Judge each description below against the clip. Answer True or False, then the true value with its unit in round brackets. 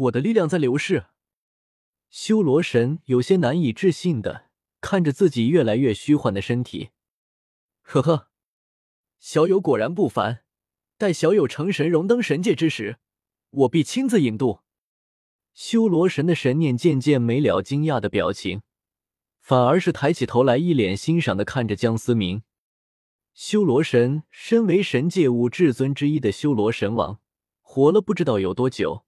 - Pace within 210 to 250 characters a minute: True (230 characters per minute)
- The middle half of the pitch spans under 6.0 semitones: False (7.0 semitones)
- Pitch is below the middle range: True (130 Hz)